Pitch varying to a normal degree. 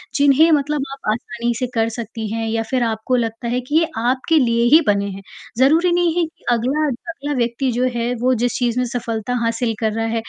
Yes: average, 3.3 semitones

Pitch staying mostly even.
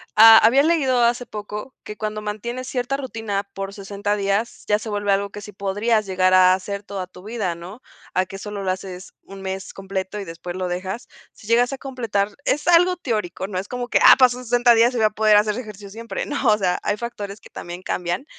No: average, 3.5 semitones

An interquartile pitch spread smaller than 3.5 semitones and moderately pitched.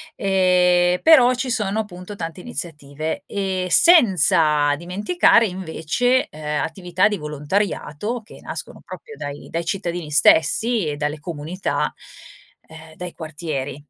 No: average, 4.8 semitones; medium, 180 Hz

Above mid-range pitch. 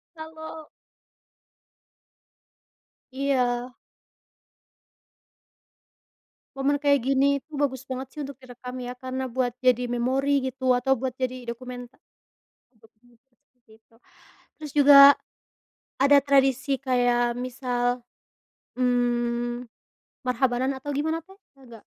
Yes: very high, 255 Hz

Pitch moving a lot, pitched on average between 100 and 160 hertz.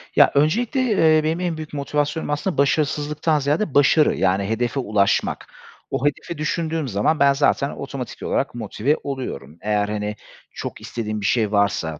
Yes: wide, 6.3 semitones; medium, 140 Hz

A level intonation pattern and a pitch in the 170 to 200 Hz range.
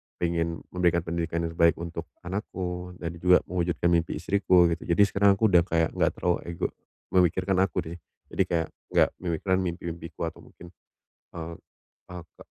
No: narrow, 1.4 semitones; very low, 85 Hz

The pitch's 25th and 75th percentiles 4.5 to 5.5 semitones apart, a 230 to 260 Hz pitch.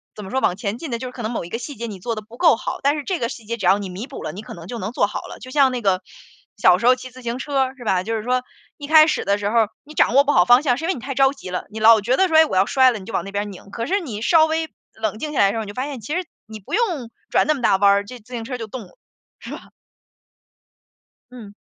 Yes: average, 4.8 semitones; high, 235 Hz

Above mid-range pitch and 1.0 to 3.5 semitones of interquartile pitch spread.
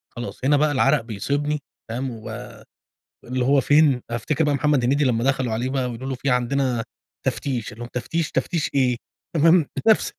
No: low, 135 Hz; average, 3.2 semitones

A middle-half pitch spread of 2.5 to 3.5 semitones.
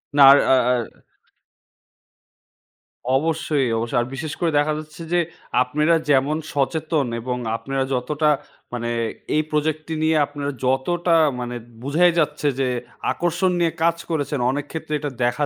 Yes: average, 3.1 semitones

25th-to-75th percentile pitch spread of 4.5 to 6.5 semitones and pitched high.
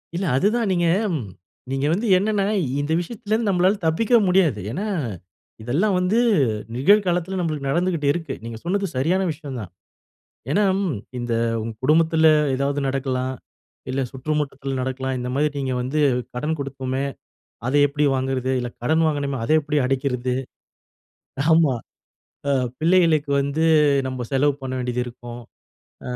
No: average, 4.8 semitones; medium, 145 Hz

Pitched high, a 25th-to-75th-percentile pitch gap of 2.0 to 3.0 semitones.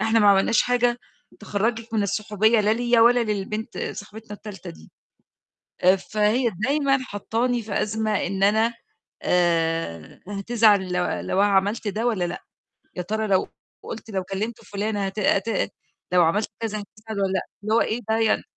Yes: high, 210 Hz; narrow, 2.5 semitones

